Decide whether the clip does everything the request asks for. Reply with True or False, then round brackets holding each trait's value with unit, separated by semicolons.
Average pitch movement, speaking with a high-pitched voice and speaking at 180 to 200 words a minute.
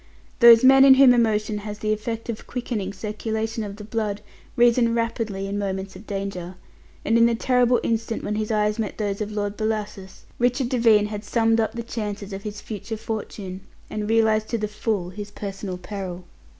False (2.1 semitones; 215 Hz; 190 wpm)